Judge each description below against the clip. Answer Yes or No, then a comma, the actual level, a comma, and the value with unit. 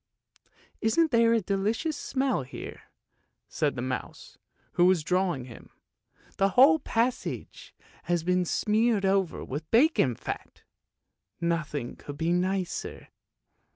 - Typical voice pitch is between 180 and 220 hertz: Yes, medium, 185 Hz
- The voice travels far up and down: Yes, wide, 6.1 semitones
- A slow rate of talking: Yes, slow, 130 wpm